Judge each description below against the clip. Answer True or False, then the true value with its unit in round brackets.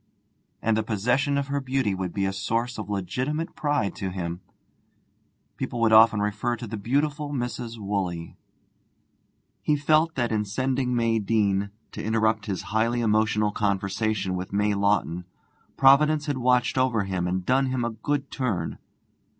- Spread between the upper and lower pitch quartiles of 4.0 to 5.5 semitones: True (4.4 semitones)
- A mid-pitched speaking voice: False (110 Hz)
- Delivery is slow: False (160 wpm)